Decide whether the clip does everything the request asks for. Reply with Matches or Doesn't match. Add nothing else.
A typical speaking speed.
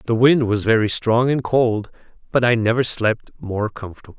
Matches